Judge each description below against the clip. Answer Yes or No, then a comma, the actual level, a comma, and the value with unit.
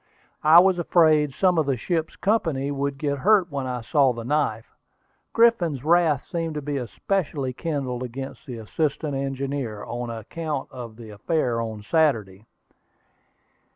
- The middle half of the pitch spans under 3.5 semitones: No, average, 4.7 semitones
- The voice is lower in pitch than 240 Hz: Yes, medium, 140 Hz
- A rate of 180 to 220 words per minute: No, average, 150 wpm